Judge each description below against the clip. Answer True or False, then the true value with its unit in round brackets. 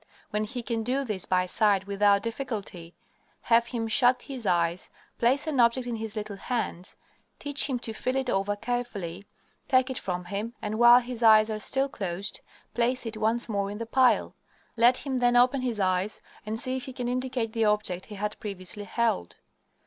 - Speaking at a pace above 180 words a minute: True (195 wpm)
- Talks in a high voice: True (225 Hz)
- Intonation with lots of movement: False (3.5 semitones)